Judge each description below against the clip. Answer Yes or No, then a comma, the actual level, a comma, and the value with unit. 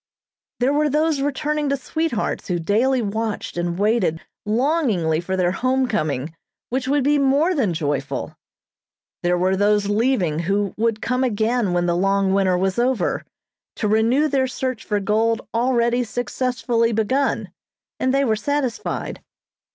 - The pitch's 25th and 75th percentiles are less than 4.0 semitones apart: No, average, 5.2 semitones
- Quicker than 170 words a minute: No, average, 150 wpm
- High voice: Yes, high, 230 Hz